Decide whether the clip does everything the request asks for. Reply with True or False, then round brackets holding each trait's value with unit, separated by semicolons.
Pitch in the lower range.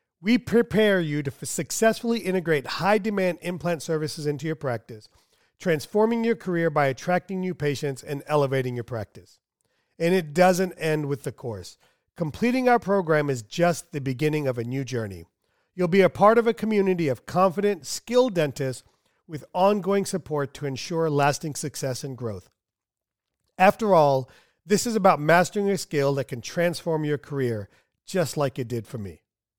False (155 Hz)